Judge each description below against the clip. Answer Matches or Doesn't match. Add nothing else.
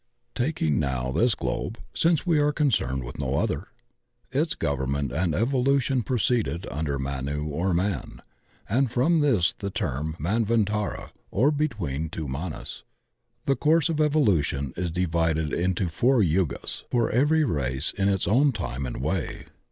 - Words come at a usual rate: Matches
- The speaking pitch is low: Matches